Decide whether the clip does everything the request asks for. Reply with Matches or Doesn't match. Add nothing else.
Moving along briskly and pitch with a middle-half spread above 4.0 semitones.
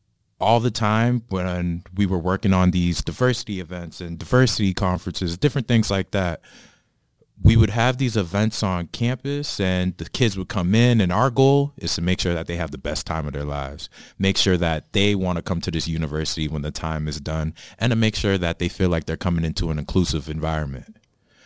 Matches